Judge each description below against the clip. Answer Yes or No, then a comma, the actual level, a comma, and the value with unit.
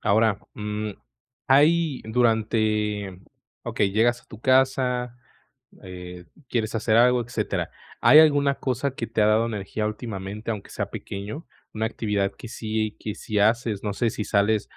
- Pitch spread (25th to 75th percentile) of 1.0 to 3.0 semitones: Yes, average, 2.7 semitones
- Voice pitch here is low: Yes, low, 110 Hz